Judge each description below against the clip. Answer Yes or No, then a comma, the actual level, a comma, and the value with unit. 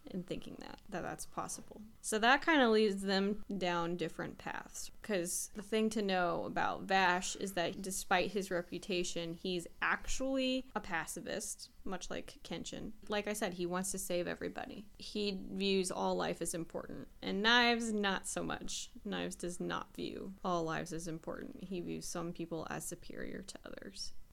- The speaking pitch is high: Yes, high, 195 Hz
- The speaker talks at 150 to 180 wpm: Yes, average, 170 wpm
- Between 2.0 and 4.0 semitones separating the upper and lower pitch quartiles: Yes, average, 3.7 semitones